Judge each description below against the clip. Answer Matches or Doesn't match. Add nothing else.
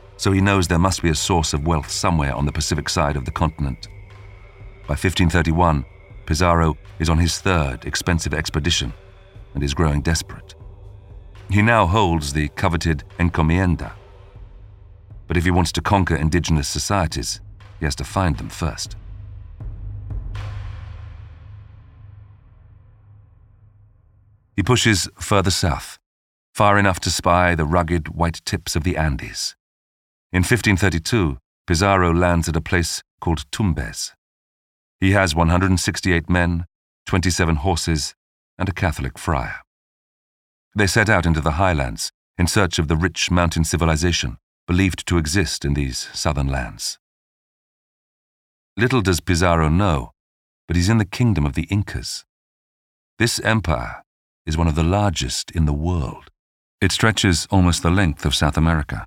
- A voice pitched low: Matches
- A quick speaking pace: Doesn't match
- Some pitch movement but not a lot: Matches